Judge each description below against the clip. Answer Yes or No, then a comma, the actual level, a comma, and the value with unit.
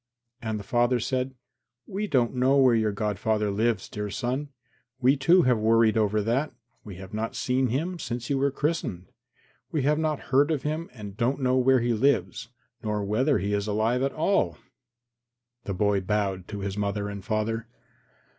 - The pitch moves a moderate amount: Yes, average, 4.3 semitones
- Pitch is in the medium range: No, low, 120 Hz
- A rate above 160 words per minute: Yes, average, 180 wpm